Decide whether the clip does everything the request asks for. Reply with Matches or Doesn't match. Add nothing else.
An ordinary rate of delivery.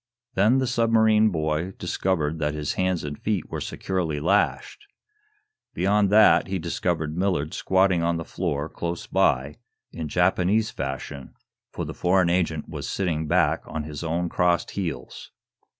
Matches